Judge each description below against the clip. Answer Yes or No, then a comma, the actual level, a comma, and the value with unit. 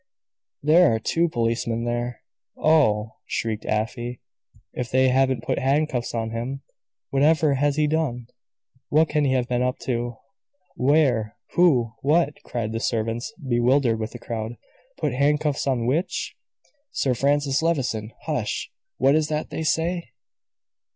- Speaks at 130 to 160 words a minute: Yes, average, 140 wpm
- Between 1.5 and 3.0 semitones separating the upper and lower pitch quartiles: No, average, 4.1 semitones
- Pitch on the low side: Yes, low, 130 Hz